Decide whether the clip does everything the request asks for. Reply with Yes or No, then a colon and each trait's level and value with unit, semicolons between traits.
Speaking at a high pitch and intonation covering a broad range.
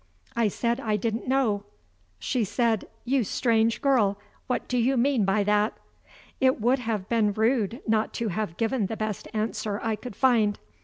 No: high, 225 Hz; average, 2.8 semitones